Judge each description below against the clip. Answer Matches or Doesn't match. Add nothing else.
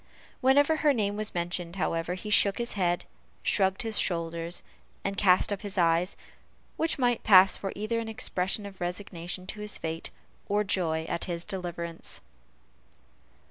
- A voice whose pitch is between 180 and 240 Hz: Matches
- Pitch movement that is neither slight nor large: Matches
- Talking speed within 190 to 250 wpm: Doesn't match